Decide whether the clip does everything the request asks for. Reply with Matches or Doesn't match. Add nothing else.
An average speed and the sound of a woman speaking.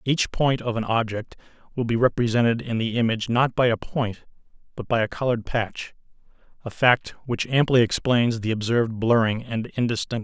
Doesn't match